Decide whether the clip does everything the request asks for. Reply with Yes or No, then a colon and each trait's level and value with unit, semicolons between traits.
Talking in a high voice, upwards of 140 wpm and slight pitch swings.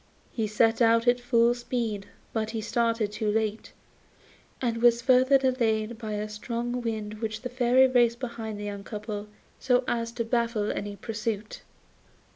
Yes: high, 230 Hz; average, 160 wpm; narrow, 2.1 semitones